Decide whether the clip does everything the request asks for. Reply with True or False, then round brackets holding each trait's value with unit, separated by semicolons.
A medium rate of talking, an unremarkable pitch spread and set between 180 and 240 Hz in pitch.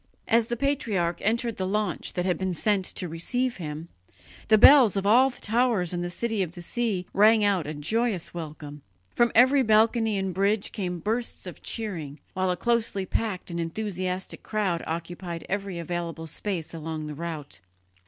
True (175 wpm; 4.6 semitones; 190 Hz)